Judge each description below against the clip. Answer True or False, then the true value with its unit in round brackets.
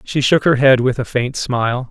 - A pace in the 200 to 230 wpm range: False (250 wpm)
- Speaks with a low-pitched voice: True (130 Hz)